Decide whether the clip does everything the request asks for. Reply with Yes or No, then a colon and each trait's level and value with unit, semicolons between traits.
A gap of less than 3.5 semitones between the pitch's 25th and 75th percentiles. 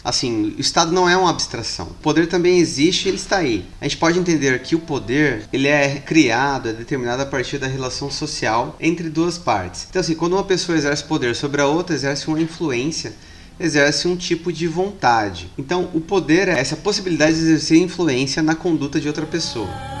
No: average, 3.8 semitones